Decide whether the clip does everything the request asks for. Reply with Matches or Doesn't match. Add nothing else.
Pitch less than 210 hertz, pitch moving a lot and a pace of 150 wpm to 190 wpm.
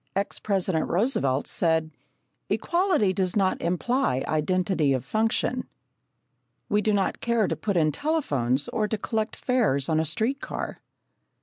Doesn't match